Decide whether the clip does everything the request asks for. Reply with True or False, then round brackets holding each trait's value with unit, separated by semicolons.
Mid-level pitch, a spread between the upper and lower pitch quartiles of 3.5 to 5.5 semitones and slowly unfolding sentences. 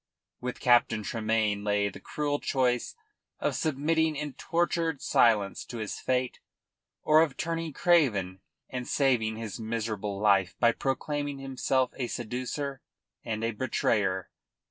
False (125 Hz; 4.9 semitones; 130 wpm)